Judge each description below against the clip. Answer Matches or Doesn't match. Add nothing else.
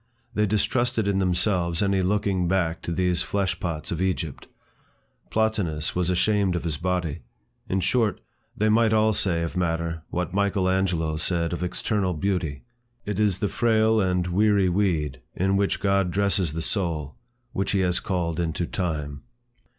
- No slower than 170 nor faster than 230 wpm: Doesn't match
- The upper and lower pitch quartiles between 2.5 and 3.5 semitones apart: Matches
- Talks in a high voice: Doesn't match